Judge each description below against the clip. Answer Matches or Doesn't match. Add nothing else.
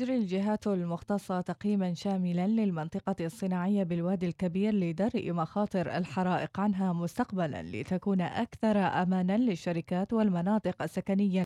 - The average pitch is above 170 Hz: Matches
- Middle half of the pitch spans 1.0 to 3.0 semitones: Matches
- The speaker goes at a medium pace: Matches